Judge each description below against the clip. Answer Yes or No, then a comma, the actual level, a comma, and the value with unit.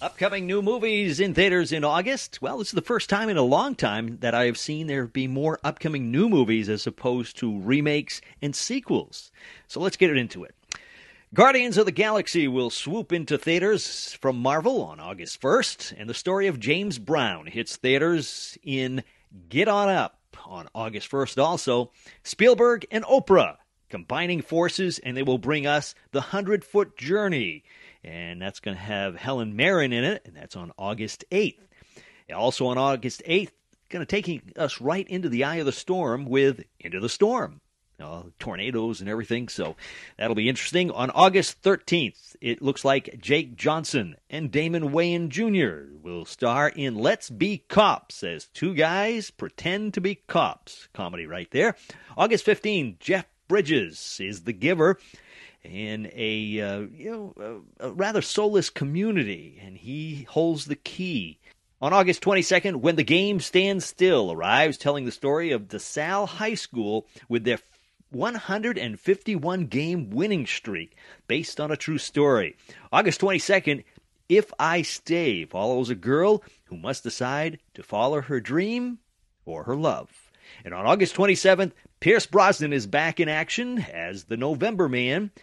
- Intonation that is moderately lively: No, wide, 7.5 semitones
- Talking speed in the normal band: Yes, average, 165 wpm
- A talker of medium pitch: Yes, medium, 155 Hz